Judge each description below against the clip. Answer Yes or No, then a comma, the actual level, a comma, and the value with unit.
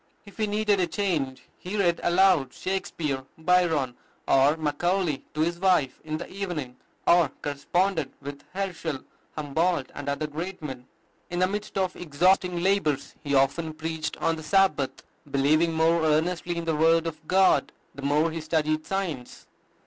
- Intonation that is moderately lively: Yes, average, 3.7 semitones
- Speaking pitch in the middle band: Yes, medium, 160 Hz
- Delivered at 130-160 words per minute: Yes, average, 155 wpm